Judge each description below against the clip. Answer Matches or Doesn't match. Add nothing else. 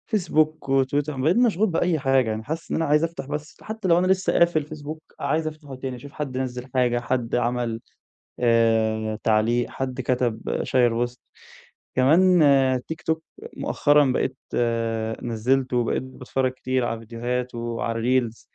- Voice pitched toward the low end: Matches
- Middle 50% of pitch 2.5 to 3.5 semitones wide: Doesn't match